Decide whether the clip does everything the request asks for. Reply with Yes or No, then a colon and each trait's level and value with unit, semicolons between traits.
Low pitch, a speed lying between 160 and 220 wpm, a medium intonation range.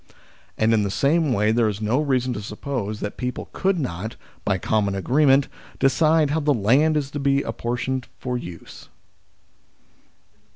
Yes: low, 125 Hz; average, 165 wpm; average, 5.0 semitones